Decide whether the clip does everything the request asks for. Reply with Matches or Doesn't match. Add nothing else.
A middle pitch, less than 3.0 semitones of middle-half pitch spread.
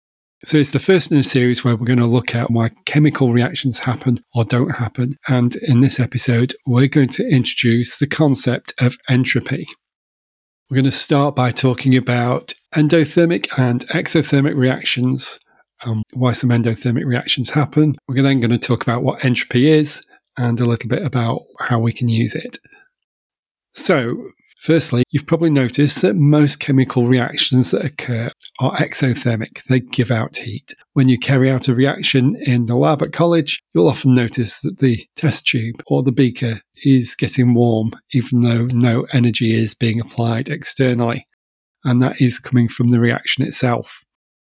Doesn't match